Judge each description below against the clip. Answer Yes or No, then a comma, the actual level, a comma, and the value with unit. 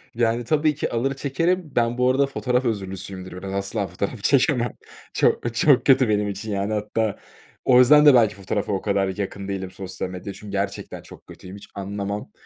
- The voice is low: Yes, low, 105 Hz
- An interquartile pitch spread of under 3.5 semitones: No, average, 4.2 semitones